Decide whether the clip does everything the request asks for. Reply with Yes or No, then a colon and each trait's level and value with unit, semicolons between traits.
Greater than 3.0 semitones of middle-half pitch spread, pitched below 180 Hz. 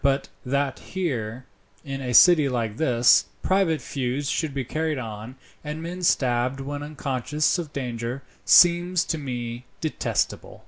Yes: average, 4.2 semitones; medium, 140 Hz